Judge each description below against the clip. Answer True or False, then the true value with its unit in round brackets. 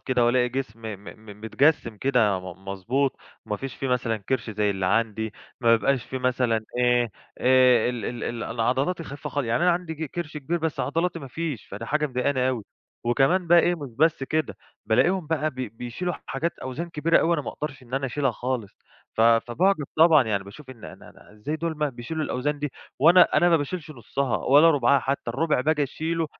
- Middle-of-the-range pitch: False (130 Hz)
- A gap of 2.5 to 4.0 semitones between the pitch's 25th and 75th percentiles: False (4.8 semitones)